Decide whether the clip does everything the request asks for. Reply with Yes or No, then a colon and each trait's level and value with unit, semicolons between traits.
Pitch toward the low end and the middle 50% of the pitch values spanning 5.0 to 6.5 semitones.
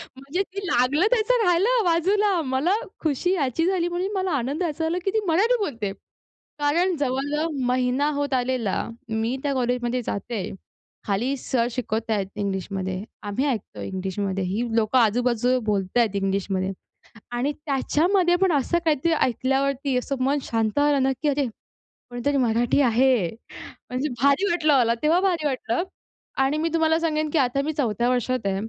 No: very high, 270 Hz; wide, 5.6 semitones